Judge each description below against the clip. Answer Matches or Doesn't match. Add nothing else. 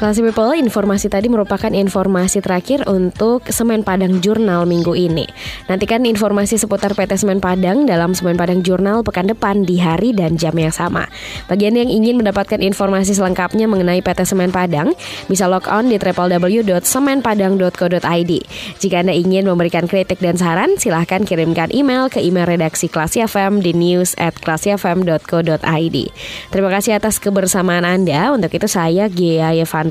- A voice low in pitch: Doesn't match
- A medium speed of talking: Doesn't match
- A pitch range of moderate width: Matches